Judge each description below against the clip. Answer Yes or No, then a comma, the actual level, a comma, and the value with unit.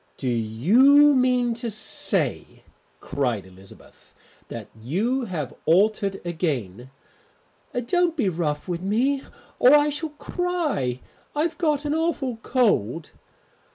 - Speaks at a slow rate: Yes, slow, 115 wpm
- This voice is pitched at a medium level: No, high, 220 Hz